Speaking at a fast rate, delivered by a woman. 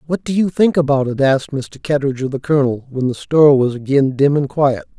No: fast, 240 wpm; male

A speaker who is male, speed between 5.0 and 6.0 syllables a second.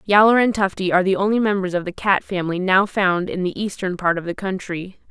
No: female; 5.9 syllables/s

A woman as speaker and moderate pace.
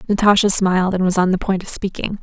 No: female; fast, 240 wpm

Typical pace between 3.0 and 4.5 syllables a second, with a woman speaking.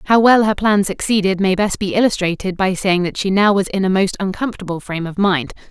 No: 6.0 syllables/s; female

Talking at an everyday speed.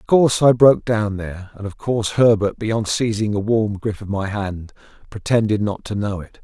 No: fast, 215 wpm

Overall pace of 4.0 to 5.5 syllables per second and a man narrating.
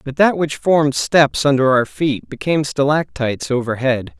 Yes: 4.9 syllables/s; male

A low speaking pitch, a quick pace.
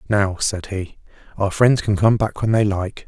Yes: low, 100 Hz; fast, 215 wpm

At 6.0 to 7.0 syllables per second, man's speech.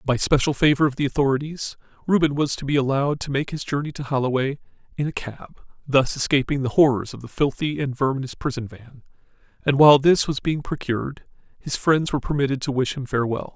Yes: 6.1 syllables/s; male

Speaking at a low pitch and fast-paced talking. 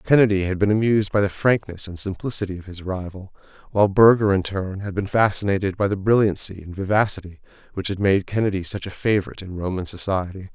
No: low, 100 Hz; average, 195 wpm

